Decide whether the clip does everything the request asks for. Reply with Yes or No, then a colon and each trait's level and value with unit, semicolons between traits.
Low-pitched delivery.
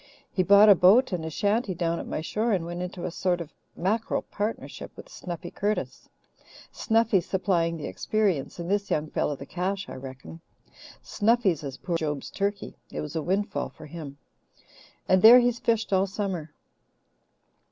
No: medium, 185 Hz